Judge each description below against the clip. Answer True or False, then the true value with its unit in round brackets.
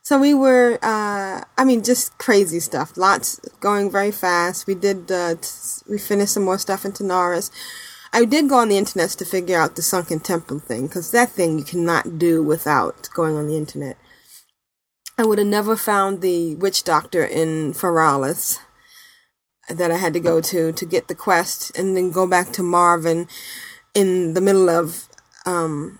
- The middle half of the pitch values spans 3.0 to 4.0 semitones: True (3.3 semitones)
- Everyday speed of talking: True (180 wpm)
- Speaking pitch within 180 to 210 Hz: True (185 Hz)